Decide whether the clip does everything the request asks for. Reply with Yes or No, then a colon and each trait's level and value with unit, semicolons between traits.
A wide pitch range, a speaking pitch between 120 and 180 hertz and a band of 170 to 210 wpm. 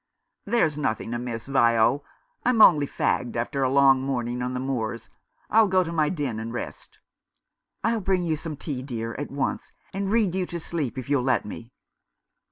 Yes: wide, 5.8 semitones; medium, 140 Hz; average, 180 wpm